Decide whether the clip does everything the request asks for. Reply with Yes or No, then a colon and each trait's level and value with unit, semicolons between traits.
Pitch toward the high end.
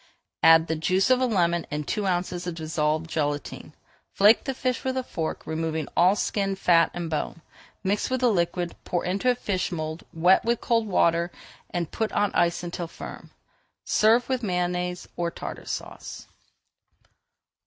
No: medium, 180 Hz